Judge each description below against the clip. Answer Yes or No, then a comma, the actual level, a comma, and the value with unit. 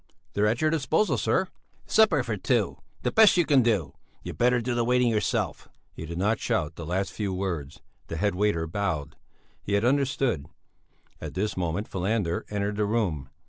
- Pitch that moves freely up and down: Yes, wide, 5.7 semitones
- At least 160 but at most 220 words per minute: Yes, average, 180 wpm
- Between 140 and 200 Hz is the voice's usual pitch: No, low, 105 Hz